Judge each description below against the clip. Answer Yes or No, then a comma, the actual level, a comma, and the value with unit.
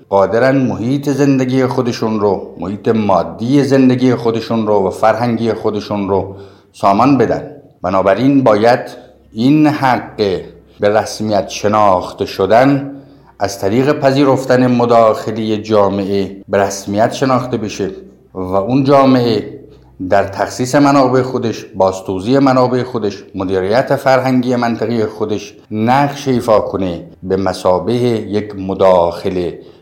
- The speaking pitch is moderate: No, low, 110 Hz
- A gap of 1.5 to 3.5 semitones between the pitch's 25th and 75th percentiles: No, average, 4.7 semitones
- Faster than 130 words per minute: No, average, 110 wpm